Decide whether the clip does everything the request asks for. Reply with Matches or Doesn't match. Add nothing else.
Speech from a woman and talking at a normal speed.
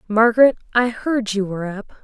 Matches